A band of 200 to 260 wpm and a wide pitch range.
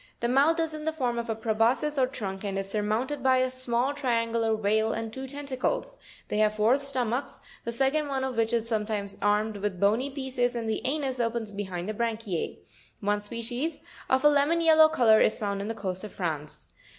No: fast, 205 wpm; average, 3.9 semitones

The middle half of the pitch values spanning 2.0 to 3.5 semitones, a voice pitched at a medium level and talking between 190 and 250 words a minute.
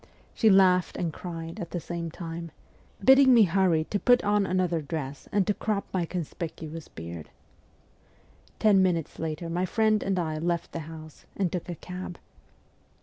No: average, 2.9 semitones; medium, 175 Hz; average, 165 wpm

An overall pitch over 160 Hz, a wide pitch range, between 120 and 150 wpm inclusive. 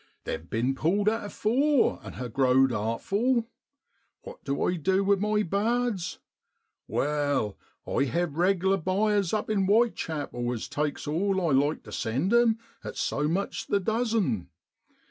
Yes: medium, 185 Hz; wide, 6.9 semitones; average, 145 wpm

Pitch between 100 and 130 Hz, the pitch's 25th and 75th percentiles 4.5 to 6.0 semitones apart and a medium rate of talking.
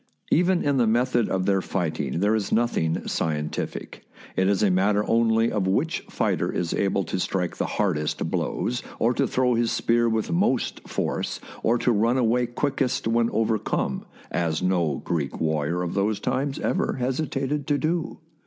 Yes: low, 110 Hz; average, 5.2 semitones; average, 170 wpm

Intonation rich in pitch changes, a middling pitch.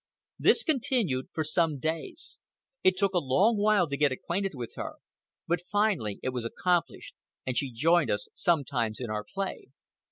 Yes: wide, 7.2 semitones; medium, 165 Hz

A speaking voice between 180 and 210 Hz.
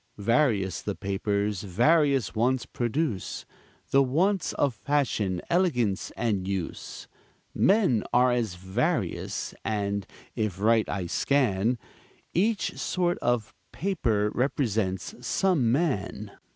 No: low, 115 Hz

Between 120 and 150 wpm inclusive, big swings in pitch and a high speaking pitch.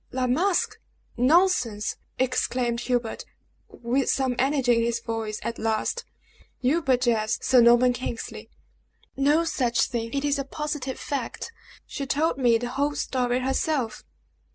No: average, 140 wpm; average, 2.9 semitones; very high, 255 Hz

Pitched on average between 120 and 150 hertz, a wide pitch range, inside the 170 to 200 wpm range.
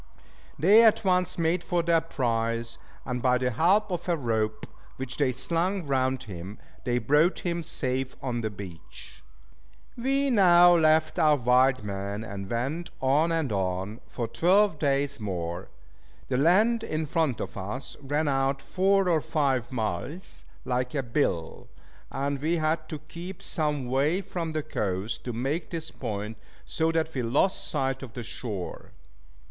No: medium, 140 Hz; wide, 6.1 semitones; average, 160 wpm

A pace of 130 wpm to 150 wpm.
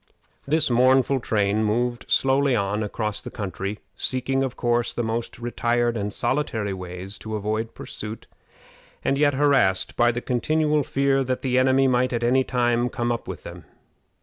No: average, 170 wpm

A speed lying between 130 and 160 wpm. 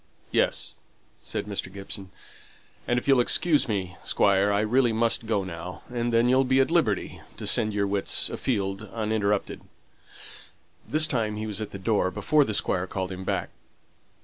No: average, 175 wpm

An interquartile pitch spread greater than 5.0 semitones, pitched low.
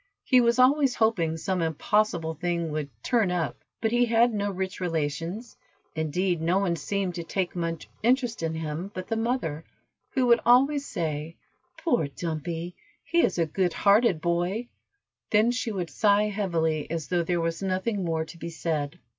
No: wide, 5.4 semitones; medium, 180 Hz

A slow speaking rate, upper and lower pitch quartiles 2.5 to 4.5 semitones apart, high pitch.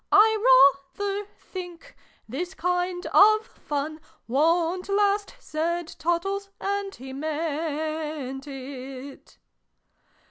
No: slow, 85 wpm; average, 5.3 semitones; very high, 340 Hz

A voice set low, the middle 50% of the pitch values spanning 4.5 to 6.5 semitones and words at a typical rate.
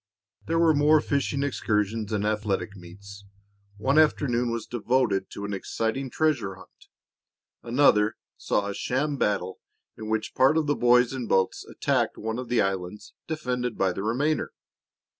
Yes: low, 115 Hz; average, 5.2 semitones; average, 155 wpm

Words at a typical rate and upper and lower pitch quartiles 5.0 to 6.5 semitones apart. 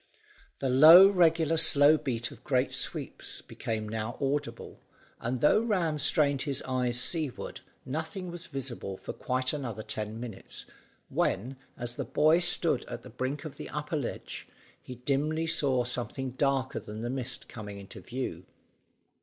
No: average, 155 wpm; average, 4.2 semitones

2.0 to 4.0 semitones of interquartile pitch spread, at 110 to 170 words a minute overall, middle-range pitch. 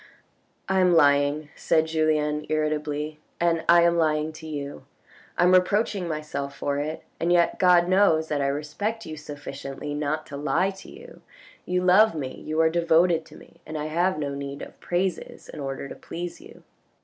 No: average, 2.8 semitones; average, 190 wpm; medium, 155 Hz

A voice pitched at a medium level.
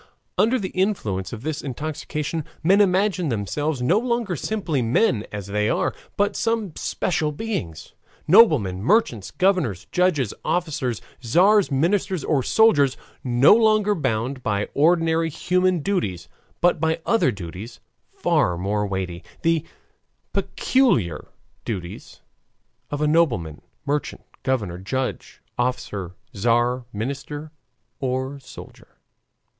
Yes: medium, 145 Hz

